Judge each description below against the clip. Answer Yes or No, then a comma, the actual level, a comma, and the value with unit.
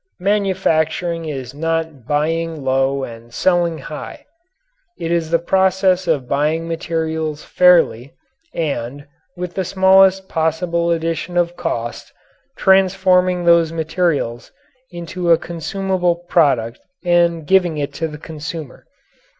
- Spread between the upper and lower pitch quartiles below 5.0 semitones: Yes, average, 2.9 semitones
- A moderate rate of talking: No, slow, 115 wpm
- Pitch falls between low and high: Yes, medium, 165 Hz